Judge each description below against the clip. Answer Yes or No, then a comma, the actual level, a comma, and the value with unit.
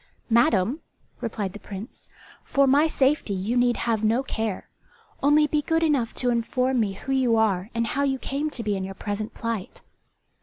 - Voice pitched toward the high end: Yes, high, 235 Hz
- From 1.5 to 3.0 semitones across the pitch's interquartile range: No, average, 4.3 semitones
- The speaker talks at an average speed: Yes, average, 185 wpm